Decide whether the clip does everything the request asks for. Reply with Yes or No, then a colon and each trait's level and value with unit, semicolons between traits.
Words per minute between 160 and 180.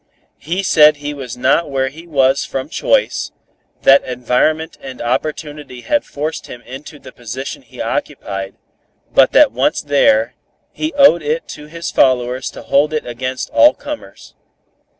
No: average, 150 wpm